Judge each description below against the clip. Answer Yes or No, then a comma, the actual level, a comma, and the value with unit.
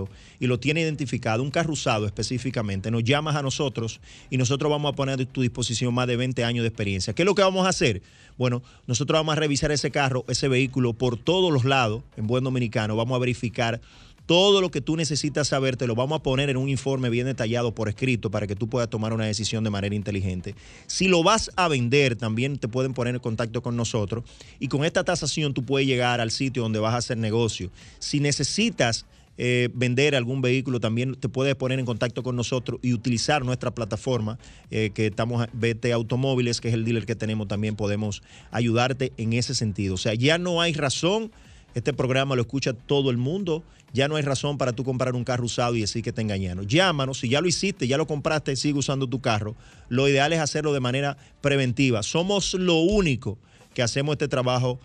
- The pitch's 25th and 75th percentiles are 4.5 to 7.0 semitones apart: No, average, 3.4 semitones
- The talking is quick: Yes, fast, 215 wpm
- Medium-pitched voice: No, low, 125 Hz